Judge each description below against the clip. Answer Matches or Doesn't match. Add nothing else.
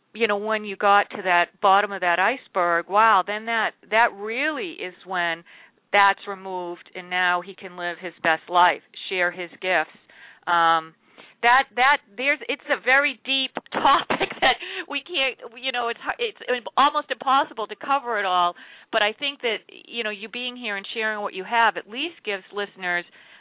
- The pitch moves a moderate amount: Doesn't match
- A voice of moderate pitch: Doesn't match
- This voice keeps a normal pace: Matches